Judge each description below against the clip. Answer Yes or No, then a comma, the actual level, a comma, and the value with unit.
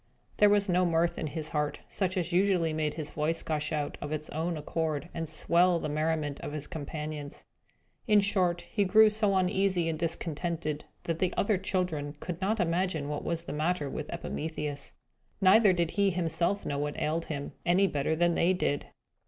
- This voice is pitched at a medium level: Yes, medium, 165 Hz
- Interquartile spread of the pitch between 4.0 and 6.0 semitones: No, average, 3.3 semitones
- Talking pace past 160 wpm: Yes, average, 185 wpm